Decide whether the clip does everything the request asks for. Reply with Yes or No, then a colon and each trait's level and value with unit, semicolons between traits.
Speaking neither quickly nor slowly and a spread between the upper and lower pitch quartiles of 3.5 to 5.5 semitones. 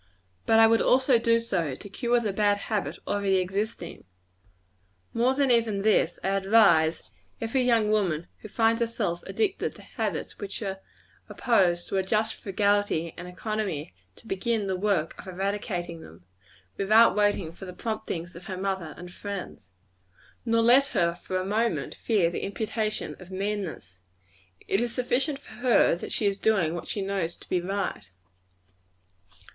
Yes: average, 160 wpm; average, 3.9 semitones